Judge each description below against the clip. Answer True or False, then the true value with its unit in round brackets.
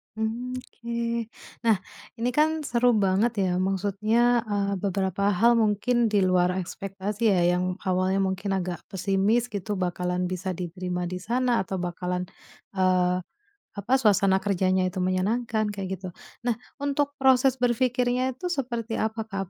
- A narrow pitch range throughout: False (4.2 semitones)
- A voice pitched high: True (200 Hz)